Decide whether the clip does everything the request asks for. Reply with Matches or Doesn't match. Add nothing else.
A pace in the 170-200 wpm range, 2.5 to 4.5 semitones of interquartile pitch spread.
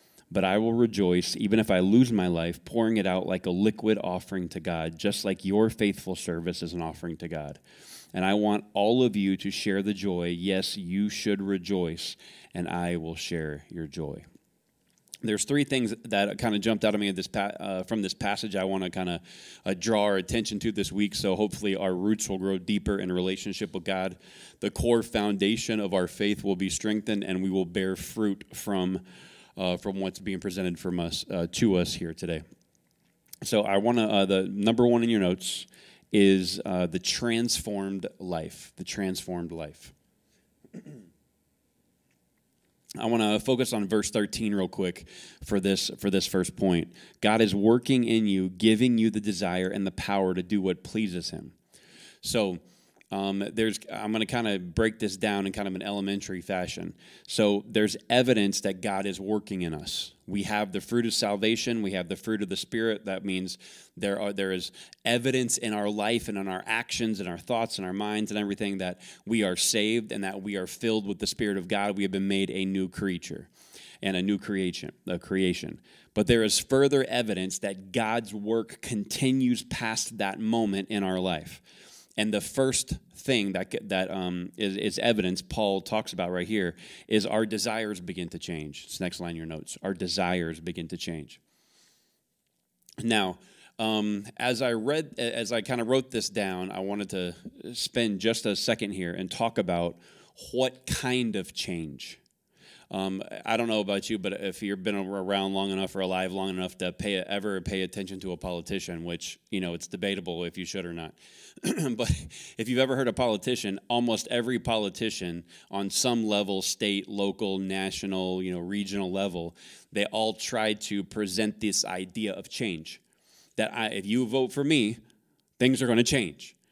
Matches